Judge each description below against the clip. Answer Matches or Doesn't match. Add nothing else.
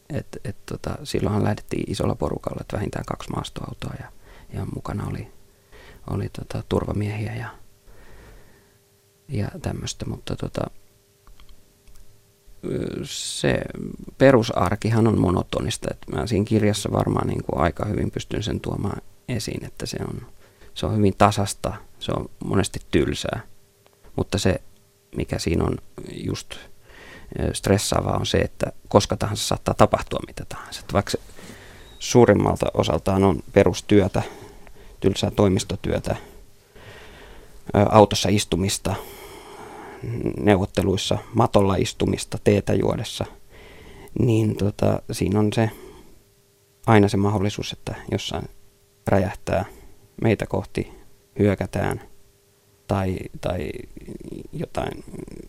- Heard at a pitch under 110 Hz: Matches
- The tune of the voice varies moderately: Doesn't match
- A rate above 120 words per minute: Doesn't match